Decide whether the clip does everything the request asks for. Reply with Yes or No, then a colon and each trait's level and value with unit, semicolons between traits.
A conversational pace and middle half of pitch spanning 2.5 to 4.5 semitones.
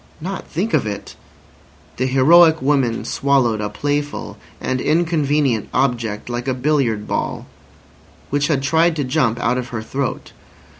Yes: average, 145 wpm; average, 3.9 semitones